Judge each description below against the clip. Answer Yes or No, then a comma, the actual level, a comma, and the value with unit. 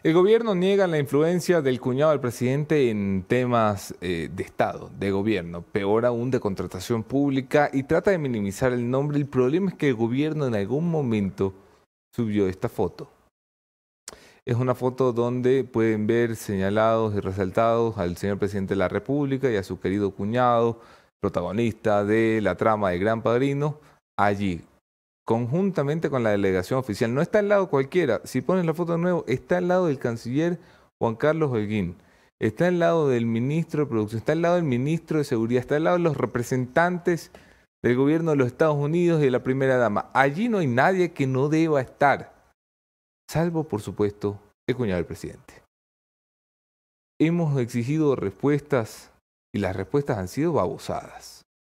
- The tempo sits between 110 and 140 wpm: No, average, 170 wpm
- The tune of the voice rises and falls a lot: Yes, wide, 6.1 semitones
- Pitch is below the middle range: Yes, low, 125 Hz